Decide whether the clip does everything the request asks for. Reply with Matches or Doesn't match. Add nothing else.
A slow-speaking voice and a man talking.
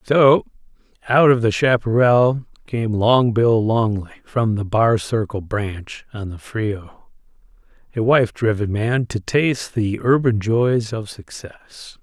Matches